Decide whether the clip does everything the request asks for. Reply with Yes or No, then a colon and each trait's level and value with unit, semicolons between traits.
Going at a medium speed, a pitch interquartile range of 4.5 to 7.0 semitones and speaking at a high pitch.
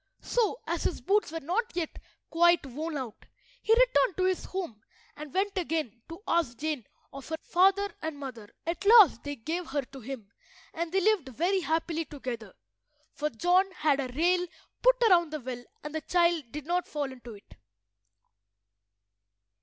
Yes: average, 170 wpm; average, 4.9 semitones; very high, 320 Hz